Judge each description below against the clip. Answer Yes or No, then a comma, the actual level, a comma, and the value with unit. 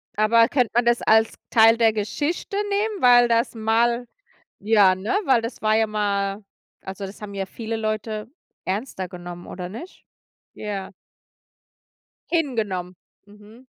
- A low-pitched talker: No, high, 220 Hz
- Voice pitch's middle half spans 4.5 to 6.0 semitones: No, average, 2.9 semitones